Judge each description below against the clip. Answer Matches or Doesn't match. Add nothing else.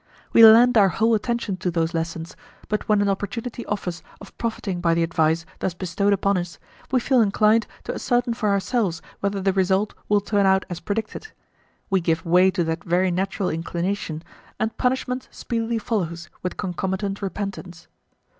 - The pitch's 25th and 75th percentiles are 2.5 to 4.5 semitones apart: Matches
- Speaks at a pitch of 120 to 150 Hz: Doesn't match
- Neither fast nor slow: Matches